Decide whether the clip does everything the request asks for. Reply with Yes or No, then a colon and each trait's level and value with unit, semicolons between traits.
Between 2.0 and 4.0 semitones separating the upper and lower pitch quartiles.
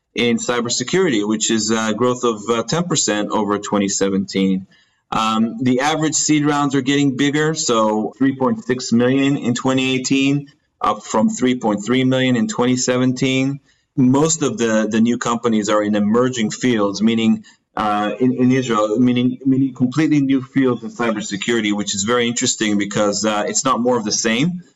Yes: average, 3.7 semitones